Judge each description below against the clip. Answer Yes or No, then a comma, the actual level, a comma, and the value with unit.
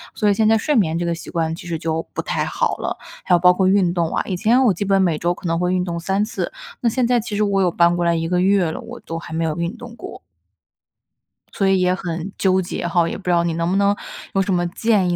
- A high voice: No, medium, 180 Hz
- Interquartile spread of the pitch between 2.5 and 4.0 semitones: Yes, average, 2.8 semitones